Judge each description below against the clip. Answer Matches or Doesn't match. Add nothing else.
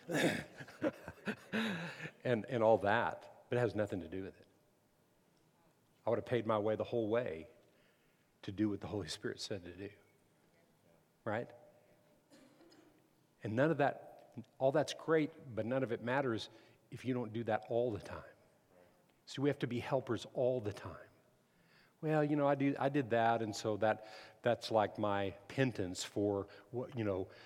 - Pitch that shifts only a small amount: Doesn't match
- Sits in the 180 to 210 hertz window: Doesn't match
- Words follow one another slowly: Doesn't match